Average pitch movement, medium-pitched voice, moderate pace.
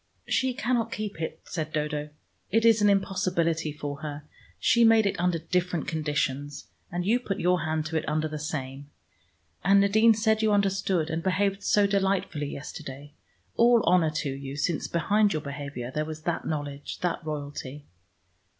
Yes: average, 5.0 semitones; medium, 165 Hz; average, 170 wpm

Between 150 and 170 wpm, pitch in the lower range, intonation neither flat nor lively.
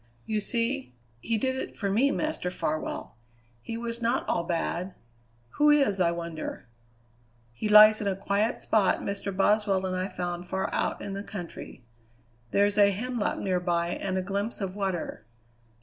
No: average, 165 wpm; high, 200 Hz; average, 3.2 semitones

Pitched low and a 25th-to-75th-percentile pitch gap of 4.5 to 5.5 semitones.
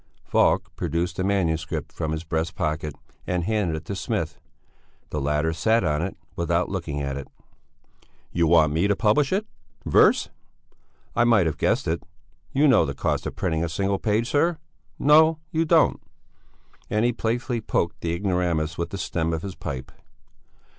Yes: very low, 85 Hz; average, 5.1 semitones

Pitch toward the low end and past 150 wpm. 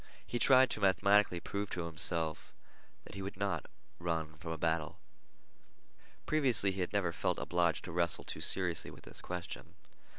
Yes: very low, 90 Hz; average, 165 wpm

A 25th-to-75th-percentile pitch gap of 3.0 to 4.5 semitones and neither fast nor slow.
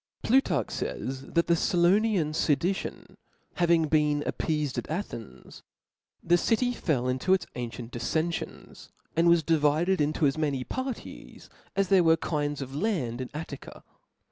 Yes: average, 3.6 semitones; average, 150 wpm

